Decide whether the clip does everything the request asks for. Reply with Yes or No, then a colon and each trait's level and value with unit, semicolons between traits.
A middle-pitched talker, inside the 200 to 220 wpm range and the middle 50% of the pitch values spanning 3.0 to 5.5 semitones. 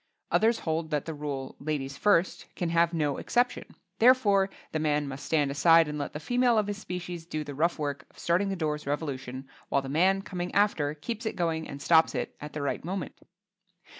Yes: medium, 160 Hz; fast, 205 wpm; average, 4.4 semitones